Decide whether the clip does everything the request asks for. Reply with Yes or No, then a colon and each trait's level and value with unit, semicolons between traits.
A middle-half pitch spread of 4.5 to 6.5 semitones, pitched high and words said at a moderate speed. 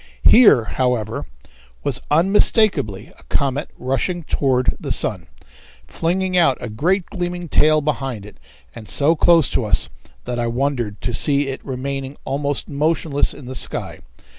No: average, 4.8 semitones; medium, 140 Hz; average, 145 wpm